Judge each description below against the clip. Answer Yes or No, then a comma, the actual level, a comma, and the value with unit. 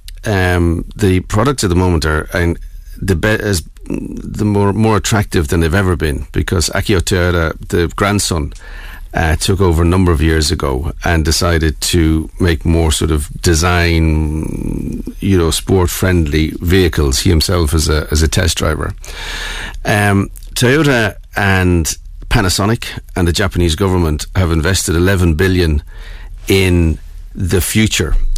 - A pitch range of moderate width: Yes, average, 3.3 semitones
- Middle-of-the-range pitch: No, very low, 90 Hz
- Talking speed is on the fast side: No, average, 145 wpm